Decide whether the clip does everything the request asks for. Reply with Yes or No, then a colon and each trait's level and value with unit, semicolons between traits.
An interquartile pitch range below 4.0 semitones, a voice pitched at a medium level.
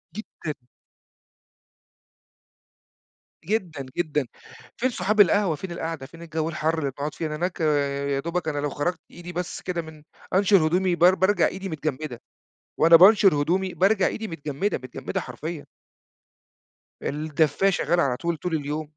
Yes: average, 3.6 semitones; medium, 165 Hz